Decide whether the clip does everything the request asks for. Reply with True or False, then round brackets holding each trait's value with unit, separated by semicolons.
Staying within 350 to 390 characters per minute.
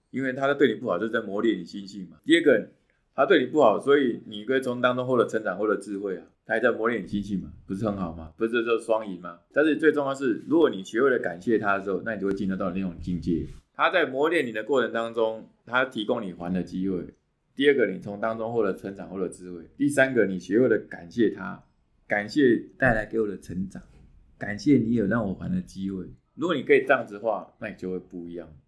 True (360 characters per minute)